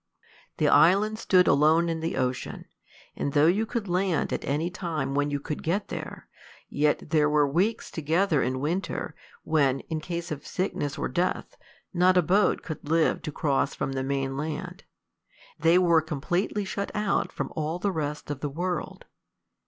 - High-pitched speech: No, medium, 160 Hz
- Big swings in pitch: No, average, 3.7 semitones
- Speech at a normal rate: Yes, average, 175 wpm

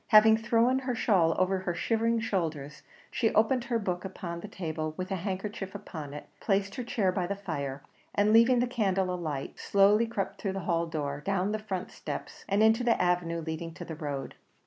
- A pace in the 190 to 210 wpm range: Yes, average, 200 wpm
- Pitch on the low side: No, high, 190 Hz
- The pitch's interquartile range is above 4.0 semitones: Yes, average, 4.6 semitones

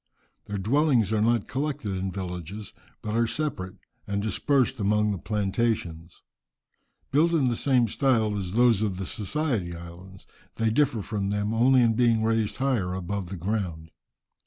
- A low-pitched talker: Yes, low, 105 Hz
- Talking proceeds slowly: No, average, 160 wpm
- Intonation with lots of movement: No, average, 4.1 semitones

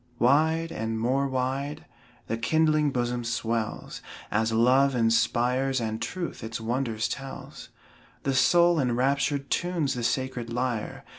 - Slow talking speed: Yes, slow, 125 wpm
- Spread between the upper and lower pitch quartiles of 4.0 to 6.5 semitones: No, average, 3.1 semitones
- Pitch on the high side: No, low, 130 Hz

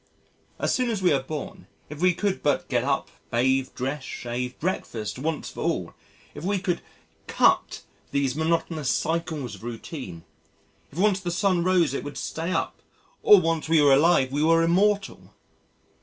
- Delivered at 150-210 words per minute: Yes, average, 170 wpm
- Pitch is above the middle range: No, medium, 160 Hz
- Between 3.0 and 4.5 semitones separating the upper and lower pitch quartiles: No, average, 5.1 semitones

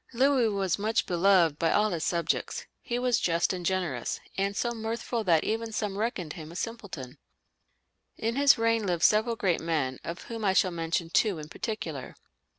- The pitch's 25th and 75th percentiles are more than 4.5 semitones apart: Yes, average, 5.1 semitones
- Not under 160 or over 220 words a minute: Yes, average, 180 wpm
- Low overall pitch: No, high, 195 Hz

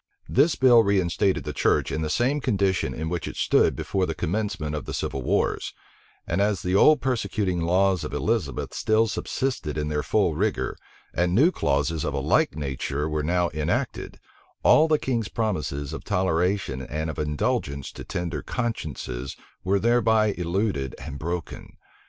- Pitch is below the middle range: Yes, very low, 90 Hz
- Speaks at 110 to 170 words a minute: Yes, average, 165 wpm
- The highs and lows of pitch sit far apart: Yes, wide, 6.1 semitones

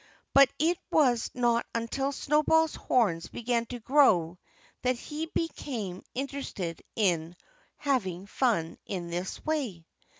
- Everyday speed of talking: No, slow, 120 wpm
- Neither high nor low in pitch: No, high, 240 Hz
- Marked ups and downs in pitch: Yes, wide, 7.3 semitones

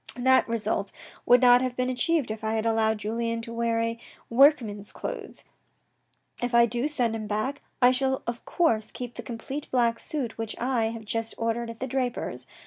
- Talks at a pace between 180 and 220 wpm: Yes, average, 190 wpm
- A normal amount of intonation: No, narrow, 2.1 semitones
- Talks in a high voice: Yes, high, 235 Hz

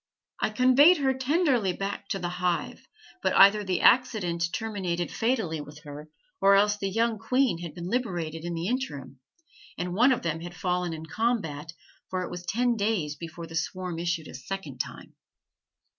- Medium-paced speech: Yes, average, 175 wpm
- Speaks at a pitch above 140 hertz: Yes, medium, 185 Hz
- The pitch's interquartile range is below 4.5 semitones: No, average, 5.2 semitones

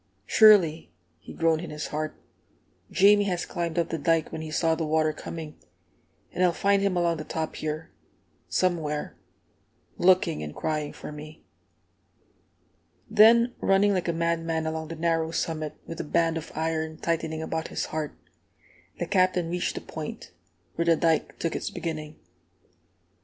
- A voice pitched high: No, medium, 165 Hz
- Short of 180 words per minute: Yes, average, 160 wpm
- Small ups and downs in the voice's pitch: Yes, narrow, 1.9 semitones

